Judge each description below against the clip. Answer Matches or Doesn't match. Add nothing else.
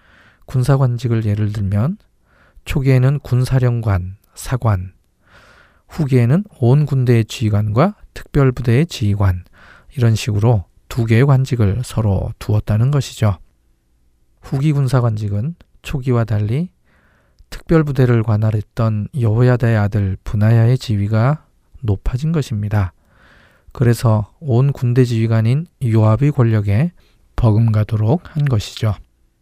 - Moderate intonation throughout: Matches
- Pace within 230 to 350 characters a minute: Matches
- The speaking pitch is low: Matches